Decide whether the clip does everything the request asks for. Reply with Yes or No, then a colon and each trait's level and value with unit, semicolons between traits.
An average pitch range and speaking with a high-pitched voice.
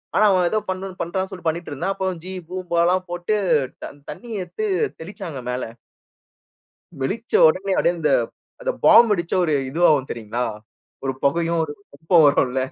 No: average, 4.2 semitones; medium, 175 Hz